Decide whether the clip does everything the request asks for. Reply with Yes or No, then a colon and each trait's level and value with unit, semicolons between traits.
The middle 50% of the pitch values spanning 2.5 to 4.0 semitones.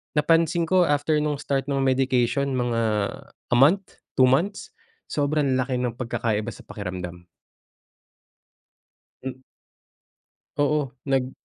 Yes: average, 3.3 semitones